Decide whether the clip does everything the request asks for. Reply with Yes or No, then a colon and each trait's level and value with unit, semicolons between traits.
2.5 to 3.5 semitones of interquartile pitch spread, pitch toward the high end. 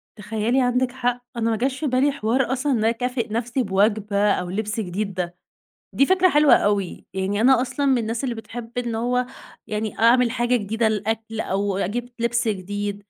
Yes: average, 3.1 semitones; high, 230 Hz